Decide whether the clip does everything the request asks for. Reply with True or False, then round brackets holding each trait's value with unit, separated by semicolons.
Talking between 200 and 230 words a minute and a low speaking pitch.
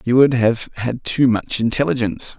False (175 wpm; 120 Hz)